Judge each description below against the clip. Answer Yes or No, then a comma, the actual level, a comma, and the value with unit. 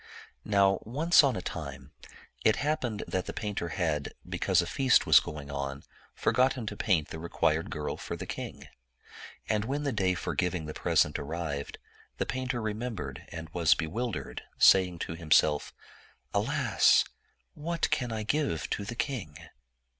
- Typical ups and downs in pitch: No, wide, 7.3 semitones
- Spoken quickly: No, average, 160 wpm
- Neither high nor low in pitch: No, very low, 95 Hz